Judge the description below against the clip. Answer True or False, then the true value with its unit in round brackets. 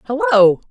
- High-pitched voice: True (200 Hz)